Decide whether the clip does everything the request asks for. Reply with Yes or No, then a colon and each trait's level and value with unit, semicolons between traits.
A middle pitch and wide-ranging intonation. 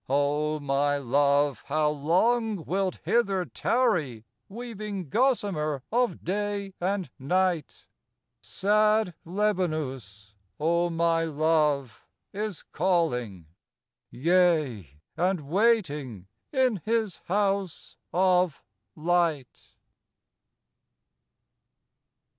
Yes: medium, 170 Hz; wide, 5.7 semitones